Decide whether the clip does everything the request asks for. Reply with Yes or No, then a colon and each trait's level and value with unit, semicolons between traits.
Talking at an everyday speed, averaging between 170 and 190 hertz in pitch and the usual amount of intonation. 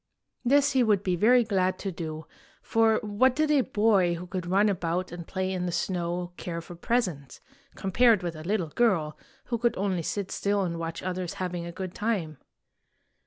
Yes: average, 190 wpm; medium, 185 Hz; average, 4.0 semitones